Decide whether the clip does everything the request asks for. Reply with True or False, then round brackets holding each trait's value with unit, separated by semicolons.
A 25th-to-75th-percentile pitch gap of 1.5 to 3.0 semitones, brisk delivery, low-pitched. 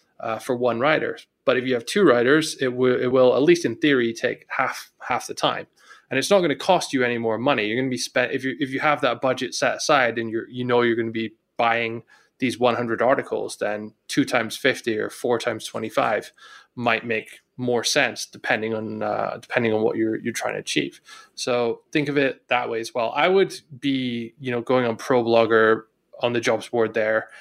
True (2.7 semitones; 230 wpm; 120 Hz)